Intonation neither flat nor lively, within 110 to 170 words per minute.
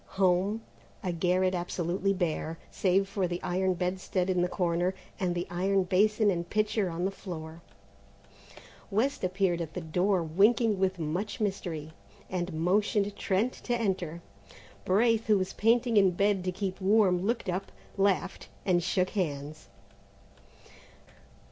No: narrow, 2.3 semitones; average, 140 wpm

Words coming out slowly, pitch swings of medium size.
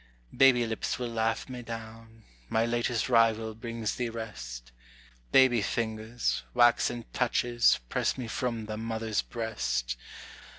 No: slow, 125 wpm; narrow, 1.4 semitones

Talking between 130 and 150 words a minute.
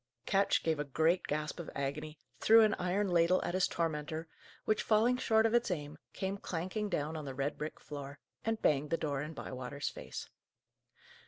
No: average, 185 wpm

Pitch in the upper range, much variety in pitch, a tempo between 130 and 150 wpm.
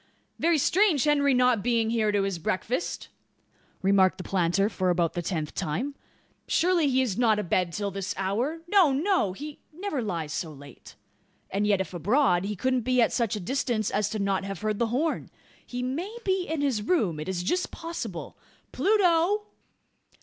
No: high, 225 Hz; wide, 7.5 semitones; average, 180 wpm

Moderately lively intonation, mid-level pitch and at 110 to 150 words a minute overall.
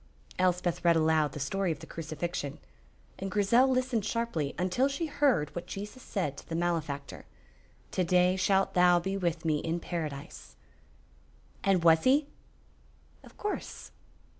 Yes: average, 3.8 semitones; medium, 180 Hz; average, 145 wpm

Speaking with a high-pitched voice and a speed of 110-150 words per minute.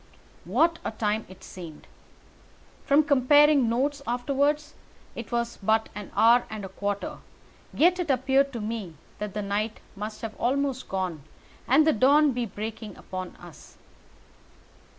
Yes: high, 235 Hz; average, 145 wpm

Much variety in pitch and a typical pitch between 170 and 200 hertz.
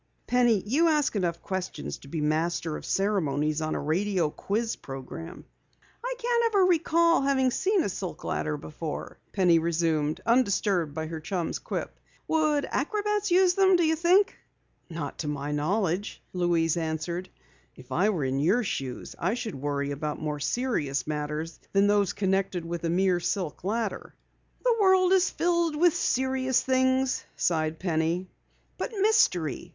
Yes: wide, 8.9 semitones; medium, 185 Hz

